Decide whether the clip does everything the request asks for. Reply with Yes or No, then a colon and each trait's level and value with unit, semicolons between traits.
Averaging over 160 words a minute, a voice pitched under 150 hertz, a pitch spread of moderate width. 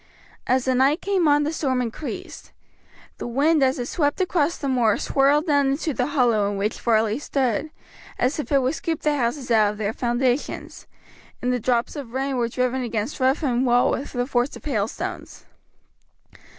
No: average, 190 wpm; very high, 260 Hz; average, 3.2 semitones